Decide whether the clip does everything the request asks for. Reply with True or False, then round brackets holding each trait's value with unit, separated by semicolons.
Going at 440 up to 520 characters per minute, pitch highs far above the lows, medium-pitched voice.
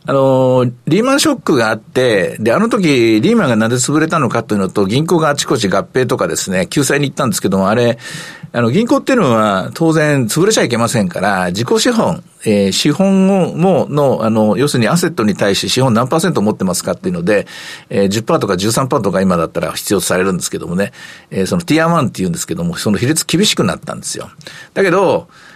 True (450 characters per minute; 7.2 semitones; 155 Hz)